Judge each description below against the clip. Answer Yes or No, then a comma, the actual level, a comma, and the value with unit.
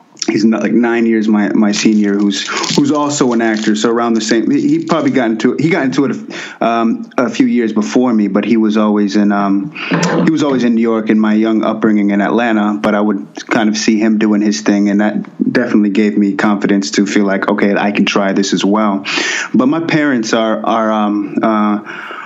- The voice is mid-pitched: No, low, 105 Hz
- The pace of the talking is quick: Yes, fast, 225 wpm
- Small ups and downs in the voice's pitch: Yes, narrow, 1.7 semitones